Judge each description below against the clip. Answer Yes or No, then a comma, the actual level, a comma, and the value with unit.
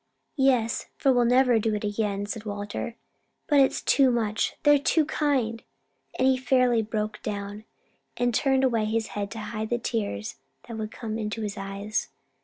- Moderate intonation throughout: Yes, average, 3.1 semitones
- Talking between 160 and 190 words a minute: Yes, average, 175 wpm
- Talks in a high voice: Yes, high, 225 Hz